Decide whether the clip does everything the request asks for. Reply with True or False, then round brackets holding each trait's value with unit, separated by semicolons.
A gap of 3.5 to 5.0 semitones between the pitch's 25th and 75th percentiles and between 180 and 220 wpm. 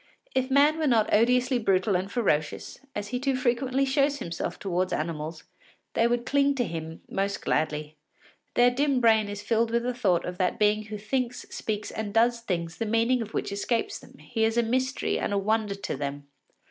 True (4.3 semitones; 200 wpm)